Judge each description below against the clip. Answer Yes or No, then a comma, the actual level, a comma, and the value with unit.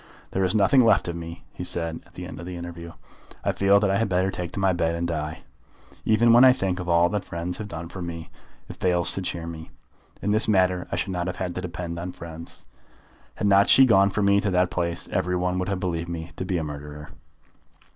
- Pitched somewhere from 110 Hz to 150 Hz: No, very low, 90 Hz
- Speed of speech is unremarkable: No, fast, 245 wpm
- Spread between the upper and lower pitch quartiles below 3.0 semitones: Yes, narrow, 2.4 semitones